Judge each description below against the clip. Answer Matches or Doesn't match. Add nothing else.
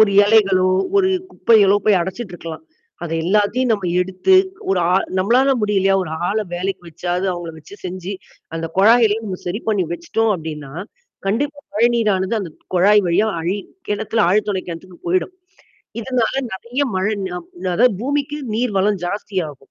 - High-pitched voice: Matches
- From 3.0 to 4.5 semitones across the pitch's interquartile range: Matches